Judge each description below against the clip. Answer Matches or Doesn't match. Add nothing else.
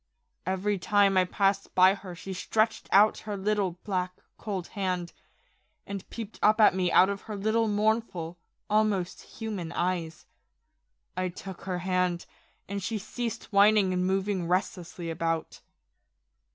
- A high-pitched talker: Matches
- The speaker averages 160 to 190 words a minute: Doesn't match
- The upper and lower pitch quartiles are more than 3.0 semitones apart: Doesn't match